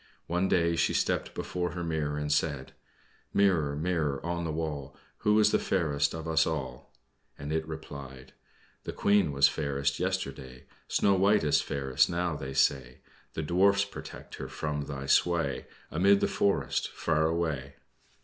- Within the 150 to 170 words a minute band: Yes, average, 160 wpm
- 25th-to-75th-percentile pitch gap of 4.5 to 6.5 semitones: No, average, 3.9 semitones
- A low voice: Yes, very low, 80 Hz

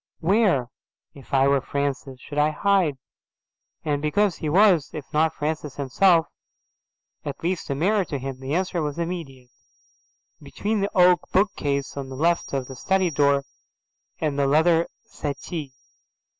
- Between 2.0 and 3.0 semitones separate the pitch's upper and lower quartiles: No, average, 4.2 semitones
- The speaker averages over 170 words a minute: No, average, 150 wpm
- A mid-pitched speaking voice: Yes, medium, 150 Hz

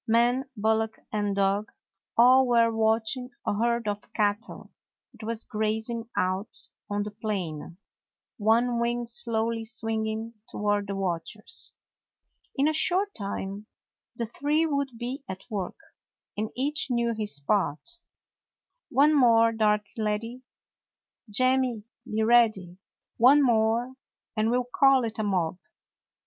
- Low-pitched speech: No, high, 225 Hz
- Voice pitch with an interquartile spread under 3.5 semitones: Yes, average, 2.7 semitones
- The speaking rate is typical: No, slow, 130 wpm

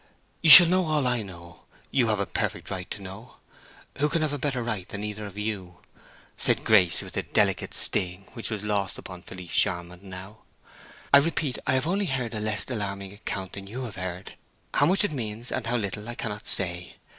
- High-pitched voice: No, low, 105 Hz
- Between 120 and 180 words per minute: No, average, 200 wpm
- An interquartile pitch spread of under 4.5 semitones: No, average, 5.0 semitones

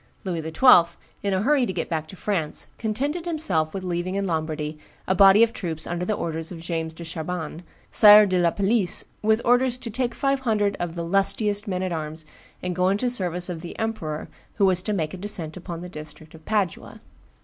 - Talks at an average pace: No, fast, 215 wpm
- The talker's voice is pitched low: No, medium, 185 Hz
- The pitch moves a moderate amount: Yes, average, 4.3 semitones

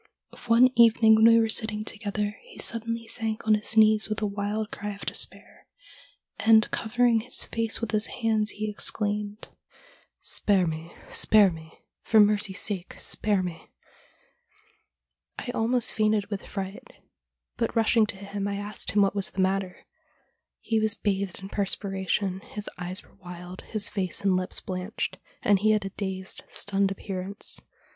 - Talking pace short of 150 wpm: No, average, 160 wpm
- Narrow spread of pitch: Yes, narrow, 2.1 semitones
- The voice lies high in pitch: Yes, high, 205 Hz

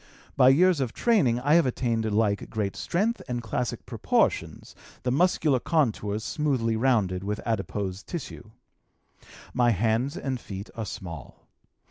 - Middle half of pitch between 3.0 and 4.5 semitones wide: No, average, 4.9 semitones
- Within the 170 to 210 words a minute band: No, slow, 135 wpm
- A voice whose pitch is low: Yes, low, 120 Hz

